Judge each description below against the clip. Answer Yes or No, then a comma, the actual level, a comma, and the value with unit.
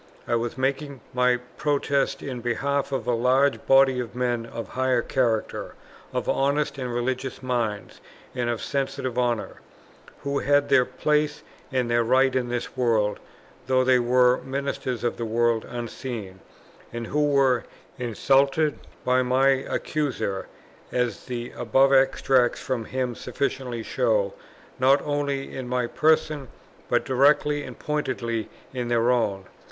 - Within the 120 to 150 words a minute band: Yes, average, 140 wpm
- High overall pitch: No, low, 130 Hz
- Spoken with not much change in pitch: Yes, narrow, 2.3 semitones